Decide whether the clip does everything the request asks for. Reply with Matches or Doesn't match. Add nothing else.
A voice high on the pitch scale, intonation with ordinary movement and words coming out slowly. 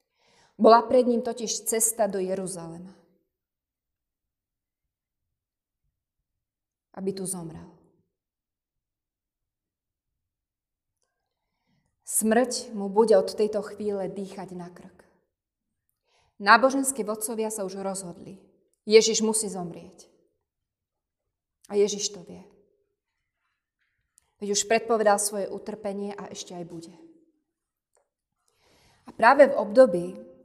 Matches